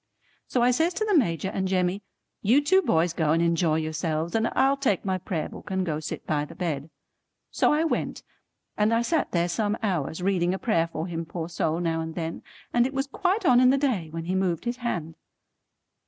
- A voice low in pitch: No, medium, 185 Hz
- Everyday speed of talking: No, fast, 220 wpm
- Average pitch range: No, wide, 6.8 semitones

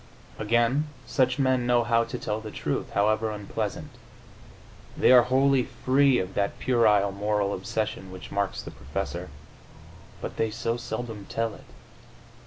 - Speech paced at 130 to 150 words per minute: Yes, average, 145 wpm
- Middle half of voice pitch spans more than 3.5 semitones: No, average, 2.9 semitones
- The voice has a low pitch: Yes, low, 115 Hz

